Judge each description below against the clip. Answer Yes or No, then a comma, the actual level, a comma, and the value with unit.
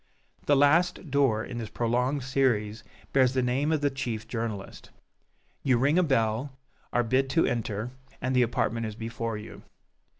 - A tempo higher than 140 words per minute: Yes, average, 165 wpm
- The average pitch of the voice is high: No, low, 125 Hz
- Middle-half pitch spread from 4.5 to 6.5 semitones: No, average, 3.2 semitones